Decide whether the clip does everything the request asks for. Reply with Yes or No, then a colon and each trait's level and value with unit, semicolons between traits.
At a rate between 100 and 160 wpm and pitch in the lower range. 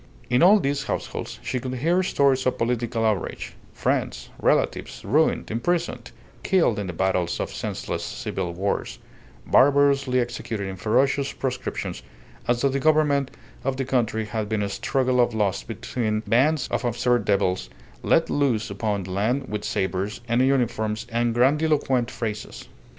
Yes: average, 150 wpm; low, 120 Hz